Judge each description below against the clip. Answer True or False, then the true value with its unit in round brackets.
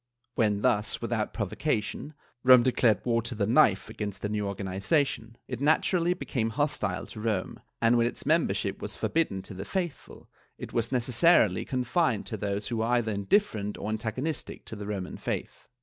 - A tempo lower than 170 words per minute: False (185 wpm)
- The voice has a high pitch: False (115 Hz)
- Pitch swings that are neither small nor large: True (3.8 semitones)